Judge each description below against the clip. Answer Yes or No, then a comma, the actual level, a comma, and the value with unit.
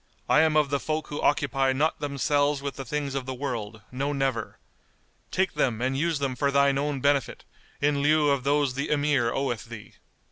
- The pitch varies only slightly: Yes, narrow, 1.8 semitones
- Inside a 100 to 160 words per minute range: No, average, 200 wpm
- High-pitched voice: No, medium, 140 Hz